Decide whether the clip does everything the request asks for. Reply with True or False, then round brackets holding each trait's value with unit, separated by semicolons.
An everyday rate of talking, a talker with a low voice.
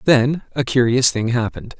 True (165 wpm; 125 Hz)